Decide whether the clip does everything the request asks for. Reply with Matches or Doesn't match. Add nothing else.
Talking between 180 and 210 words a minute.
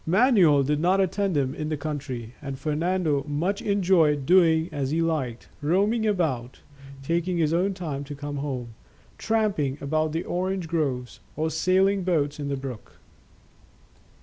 Doesn't match